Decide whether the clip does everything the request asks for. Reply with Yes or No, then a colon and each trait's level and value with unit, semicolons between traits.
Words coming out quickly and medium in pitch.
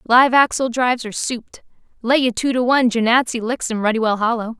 No: fast, 210 wpm; high, 240 Hz